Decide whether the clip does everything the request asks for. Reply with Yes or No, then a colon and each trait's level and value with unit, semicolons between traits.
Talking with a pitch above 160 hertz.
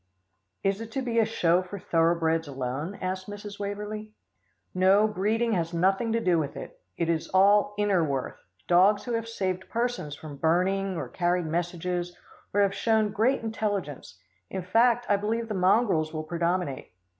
Yes: high, 190 Hz